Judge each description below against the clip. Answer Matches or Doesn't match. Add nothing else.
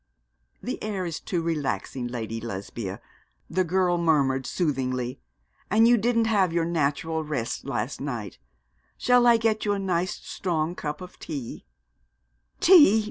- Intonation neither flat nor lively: Doesn't match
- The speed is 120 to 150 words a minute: Matches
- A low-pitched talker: Doesn't match